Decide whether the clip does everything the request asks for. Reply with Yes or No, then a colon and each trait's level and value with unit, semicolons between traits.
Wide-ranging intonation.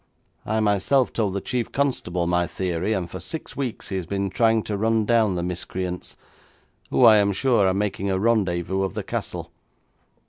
No: average, 3.3 semitones